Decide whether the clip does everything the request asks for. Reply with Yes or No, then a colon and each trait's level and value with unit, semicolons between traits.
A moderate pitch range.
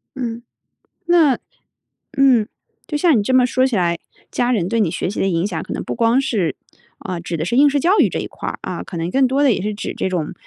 No: wide, 6.5 semitones